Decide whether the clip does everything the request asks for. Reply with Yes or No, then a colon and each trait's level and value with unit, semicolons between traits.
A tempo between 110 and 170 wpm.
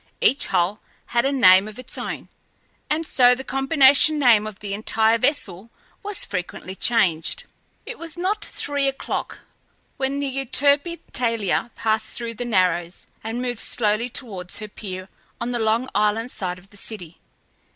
Yes: average, 160 wpm